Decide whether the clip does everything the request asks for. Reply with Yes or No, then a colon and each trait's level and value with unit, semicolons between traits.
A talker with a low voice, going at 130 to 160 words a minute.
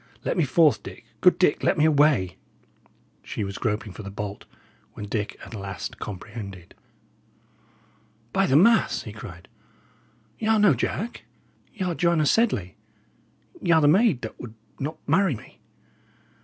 No: medium, 145 Hz; average, 155 wpm